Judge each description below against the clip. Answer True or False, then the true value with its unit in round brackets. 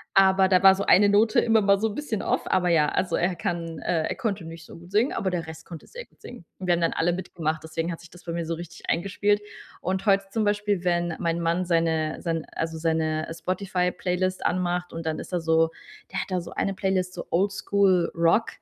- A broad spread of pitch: False (2.8 semitones)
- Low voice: False (180 Hz)